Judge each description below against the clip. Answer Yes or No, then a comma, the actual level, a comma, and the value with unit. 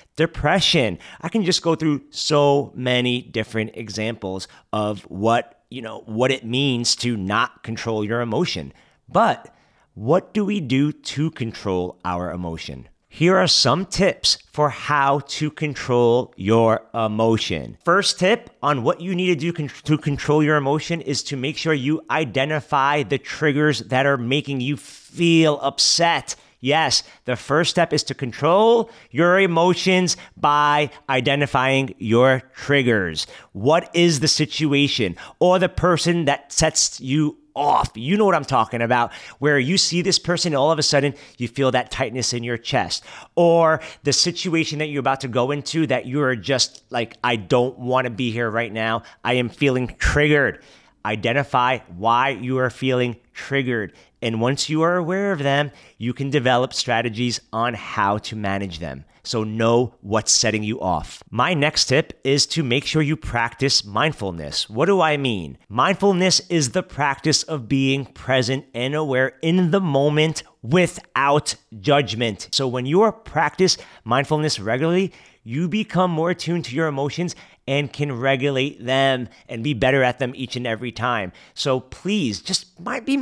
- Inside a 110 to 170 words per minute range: Yes, average, 165 wpm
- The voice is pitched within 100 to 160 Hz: Yes, low, 135 Hz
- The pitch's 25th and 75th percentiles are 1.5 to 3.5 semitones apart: No, average, 4.7 semitones